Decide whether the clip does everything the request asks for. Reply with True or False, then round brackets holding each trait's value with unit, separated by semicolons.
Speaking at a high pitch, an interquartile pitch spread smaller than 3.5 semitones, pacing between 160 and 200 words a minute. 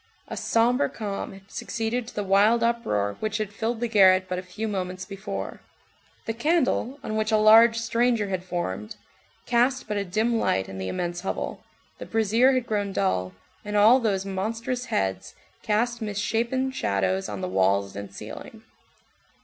False (210 Hz; 4.1 semitones; 170 wpm)